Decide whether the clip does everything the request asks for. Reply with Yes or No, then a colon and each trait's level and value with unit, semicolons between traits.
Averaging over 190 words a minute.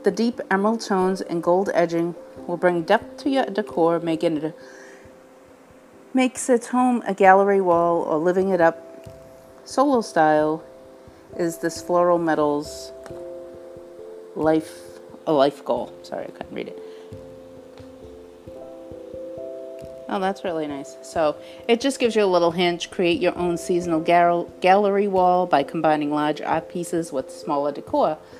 No: average, 145 wpm